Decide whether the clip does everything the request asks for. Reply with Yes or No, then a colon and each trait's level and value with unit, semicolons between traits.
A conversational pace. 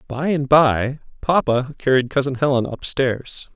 Yes: average, 150 wpm